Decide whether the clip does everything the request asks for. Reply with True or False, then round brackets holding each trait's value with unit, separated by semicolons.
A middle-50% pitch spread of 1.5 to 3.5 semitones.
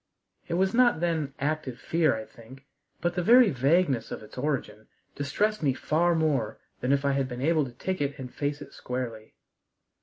False (4.7 semitones)